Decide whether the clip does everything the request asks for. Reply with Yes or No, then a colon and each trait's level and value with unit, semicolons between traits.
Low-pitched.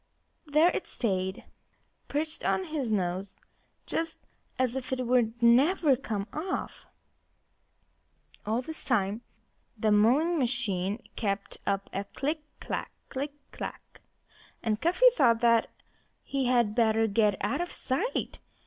No: high, 240 Hz